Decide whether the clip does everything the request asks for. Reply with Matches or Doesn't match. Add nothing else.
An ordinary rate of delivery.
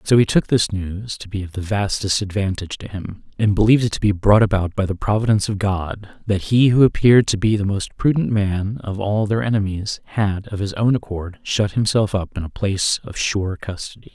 Doesn't match